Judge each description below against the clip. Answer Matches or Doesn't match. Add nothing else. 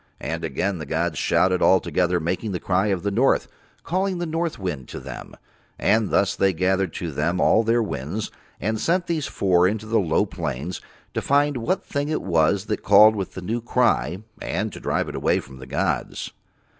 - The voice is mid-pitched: Doesn't match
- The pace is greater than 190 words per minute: Matches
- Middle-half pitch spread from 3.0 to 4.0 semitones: Doesn't match